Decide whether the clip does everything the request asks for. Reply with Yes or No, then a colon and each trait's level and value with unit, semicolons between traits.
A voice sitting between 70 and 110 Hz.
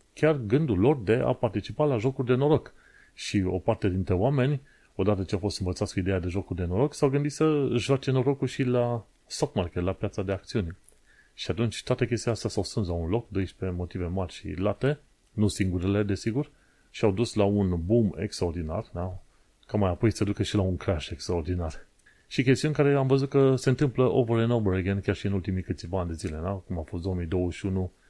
Yes: low, 105 Hz